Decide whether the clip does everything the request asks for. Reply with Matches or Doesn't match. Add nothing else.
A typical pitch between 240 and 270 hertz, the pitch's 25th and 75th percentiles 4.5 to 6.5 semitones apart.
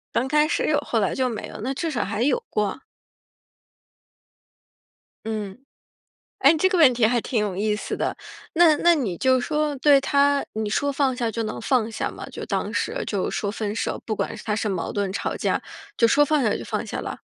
Matches